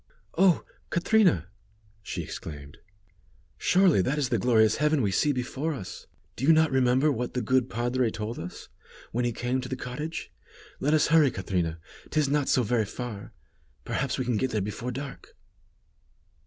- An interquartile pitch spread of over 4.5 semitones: Yes, average, 5.0 semitones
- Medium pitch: No, low, 125 Hz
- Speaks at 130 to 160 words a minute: No, average, 170 wpm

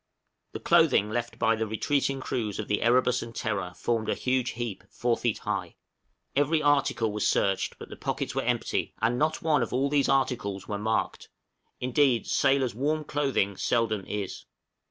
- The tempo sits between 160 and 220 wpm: Yes, average, 175 wpm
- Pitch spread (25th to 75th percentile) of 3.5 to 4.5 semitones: Yes, average, 4.0 semitones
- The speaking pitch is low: Yes, low, 120 Hz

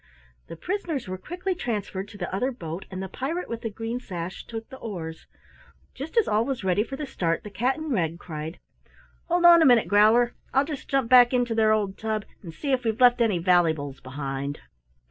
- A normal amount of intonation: No, wide, 6.3 semitones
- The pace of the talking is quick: Yes, fast, 210 wpm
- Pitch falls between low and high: No, high, 220 Hz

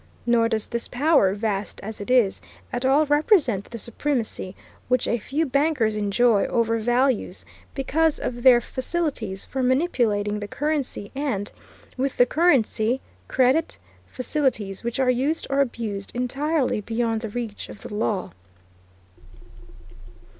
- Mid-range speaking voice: No, high, 245 Hz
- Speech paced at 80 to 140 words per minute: Yes, slow, 135 wpm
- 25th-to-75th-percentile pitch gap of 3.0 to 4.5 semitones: Yes, average, 4.1 semitones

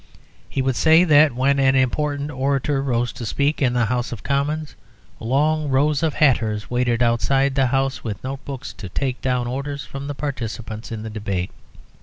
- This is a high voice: No, low, 135 Hz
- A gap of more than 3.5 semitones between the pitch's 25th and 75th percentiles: No, average, 2.8 semitones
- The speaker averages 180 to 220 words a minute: Yes, average, 185 wpm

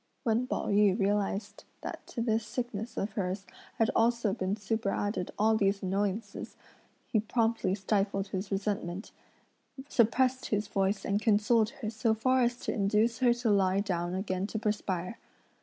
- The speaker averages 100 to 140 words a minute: No, average, 155 wpm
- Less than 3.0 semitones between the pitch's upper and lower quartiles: Yes, narrow, 2.4 semitones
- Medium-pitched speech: No, high, 210 Hz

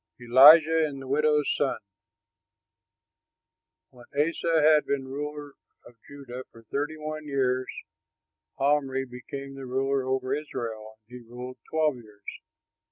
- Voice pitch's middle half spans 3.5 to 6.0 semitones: No, average, 2.9 semitones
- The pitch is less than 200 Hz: Yes, low, 135 Hz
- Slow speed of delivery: Yes, slow, 120 wpm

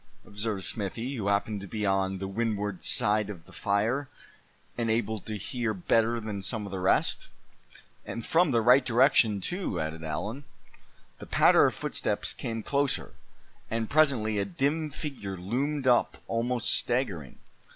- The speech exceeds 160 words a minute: No, average, 155 wpm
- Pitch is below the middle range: Yes, low, 110 Hz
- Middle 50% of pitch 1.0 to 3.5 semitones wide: No, average, 3.9 semitones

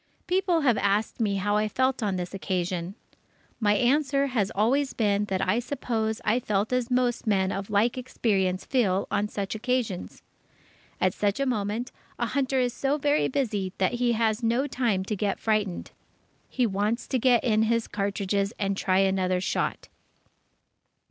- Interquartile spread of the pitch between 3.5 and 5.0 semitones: Yes, average, 4.1 semitones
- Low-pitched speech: No, high, 215 Hz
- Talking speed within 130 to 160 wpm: No, average, 170 wpm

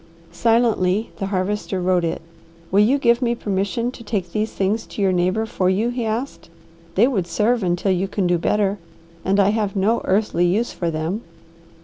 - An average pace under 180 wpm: No, average, 190 wpm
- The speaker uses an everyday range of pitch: Yes, average, 3.3 semitones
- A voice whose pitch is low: No, high, 200 Hz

